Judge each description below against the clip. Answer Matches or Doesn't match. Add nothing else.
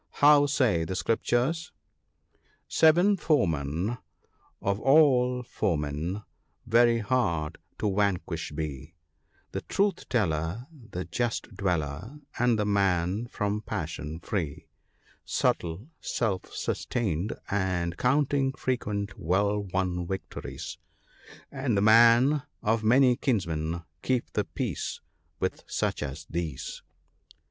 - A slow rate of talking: Matches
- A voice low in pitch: Matches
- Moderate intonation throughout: Doesn't match